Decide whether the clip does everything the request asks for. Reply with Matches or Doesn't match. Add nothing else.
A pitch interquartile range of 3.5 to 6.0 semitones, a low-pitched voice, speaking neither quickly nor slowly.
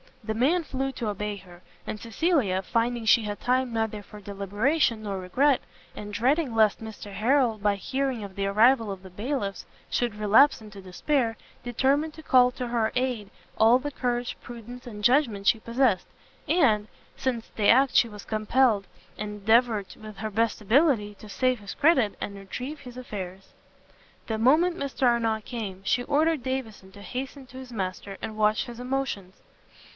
Doesn't match